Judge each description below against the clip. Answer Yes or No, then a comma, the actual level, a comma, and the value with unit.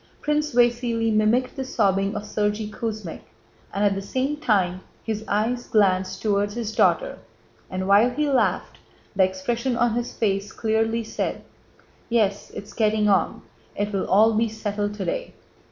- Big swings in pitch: No, average, 2.8 semitones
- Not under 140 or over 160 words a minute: Yes, average, 155 wpm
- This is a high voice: Yes, high, 215 Hz